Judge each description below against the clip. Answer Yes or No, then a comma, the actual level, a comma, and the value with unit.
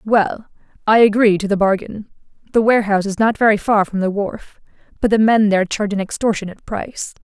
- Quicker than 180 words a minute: Yes, average, 190 wpm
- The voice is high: Yes, high, 205 Hz